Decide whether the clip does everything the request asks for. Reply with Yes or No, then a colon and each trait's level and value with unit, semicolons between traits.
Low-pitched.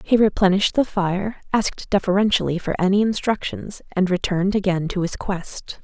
No: high, 195 Hz